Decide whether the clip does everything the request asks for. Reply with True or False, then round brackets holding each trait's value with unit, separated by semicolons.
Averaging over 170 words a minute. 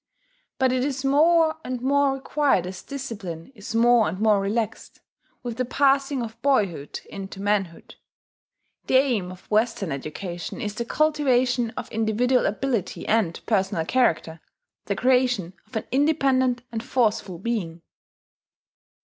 False (135 wpm)